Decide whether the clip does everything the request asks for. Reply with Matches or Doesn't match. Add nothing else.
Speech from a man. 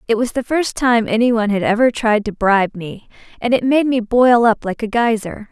Doesn't match